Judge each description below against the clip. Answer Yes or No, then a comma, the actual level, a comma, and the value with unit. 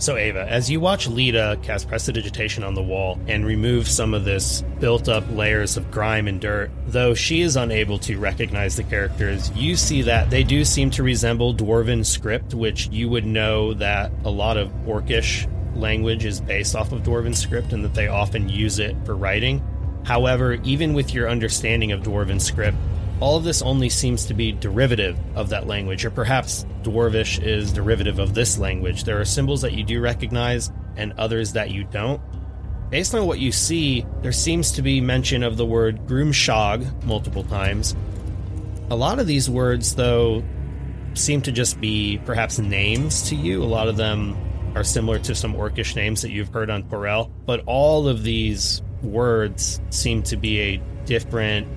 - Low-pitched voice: Yes, low, 110 Hz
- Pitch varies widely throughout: No, average, 3.0 semitones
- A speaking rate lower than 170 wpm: No, average, 185 wpm